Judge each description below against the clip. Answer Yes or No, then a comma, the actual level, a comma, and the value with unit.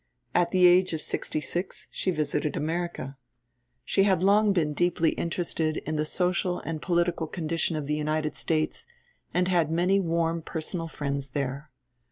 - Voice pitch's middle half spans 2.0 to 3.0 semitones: Yes, narrow, 2.6 semitones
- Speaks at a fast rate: No, average, 160 wpm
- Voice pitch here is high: No, medium, 165 Hz